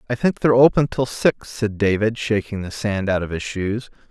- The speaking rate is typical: No, fast, 220 wpm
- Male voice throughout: Yes, male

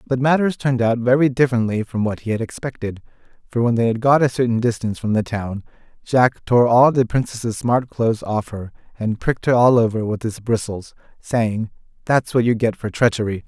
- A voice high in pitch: No, low, 115 Hz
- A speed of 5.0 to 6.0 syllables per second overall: Yes, 5.5 syllables/s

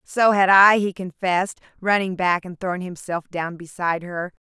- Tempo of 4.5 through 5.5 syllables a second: Yes, 4.9 syllables/s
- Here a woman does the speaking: Yes, female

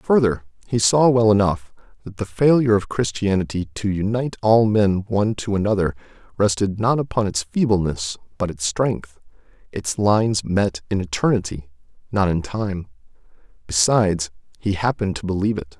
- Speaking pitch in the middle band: No, low, 100 Hz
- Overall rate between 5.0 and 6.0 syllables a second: Yes, 5.2 syllables/s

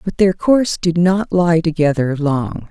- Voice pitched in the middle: Yes, medium, 175 Hz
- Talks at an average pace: Yes, average, 180 wpm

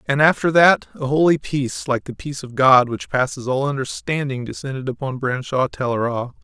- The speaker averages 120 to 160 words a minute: No, average, 175 wpm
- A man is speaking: Yes, male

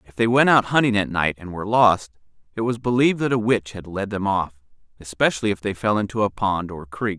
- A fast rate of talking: Yes, fast, 240 wpm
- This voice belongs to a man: Yes, male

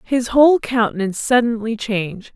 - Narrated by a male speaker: No, female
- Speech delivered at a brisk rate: No, slow, 125 wpm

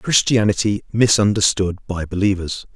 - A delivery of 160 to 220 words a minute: No, slow, 85 wpm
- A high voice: No, low, 100 Hz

